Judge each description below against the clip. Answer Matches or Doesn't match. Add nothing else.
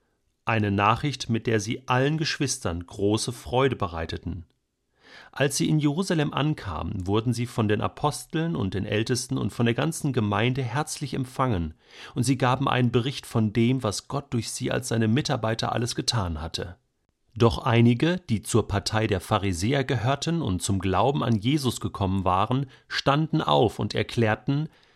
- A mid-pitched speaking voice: Doesn't match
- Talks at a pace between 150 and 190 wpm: Matches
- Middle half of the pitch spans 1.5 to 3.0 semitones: Doesn't match